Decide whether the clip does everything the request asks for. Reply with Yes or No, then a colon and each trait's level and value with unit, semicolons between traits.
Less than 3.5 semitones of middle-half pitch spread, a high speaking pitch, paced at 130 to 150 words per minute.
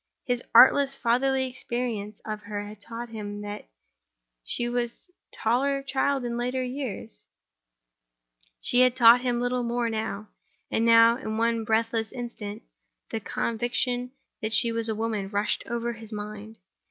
Yes: narrow, 2.6 semitones; high, 230 Hz; average, 140 wpm